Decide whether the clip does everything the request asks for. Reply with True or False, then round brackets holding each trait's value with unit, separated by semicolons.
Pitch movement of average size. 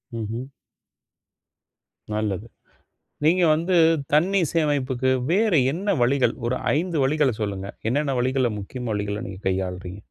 False (6.9 semitones)